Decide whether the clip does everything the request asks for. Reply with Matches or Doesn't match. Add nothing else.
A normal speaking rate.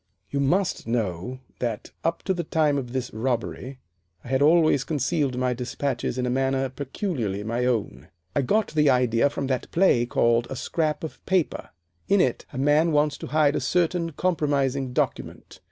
Matches